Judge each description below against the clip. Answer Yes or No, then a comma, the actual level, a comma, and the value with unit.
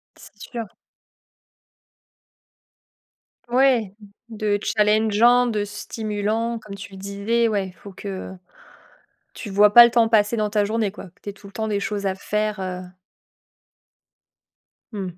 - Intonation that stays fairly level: Yes, narrow, 1.9 semitones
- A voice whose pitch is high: Yes, high, 210 Hz